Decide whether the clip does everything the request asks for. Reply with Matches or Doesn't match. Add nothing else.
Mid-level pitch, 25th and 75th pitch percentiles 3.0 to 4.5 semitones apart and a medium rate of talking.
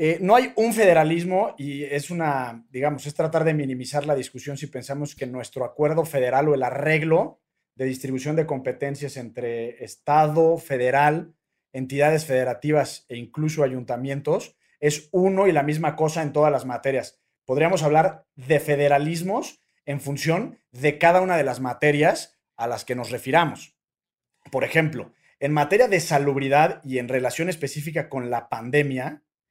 Matches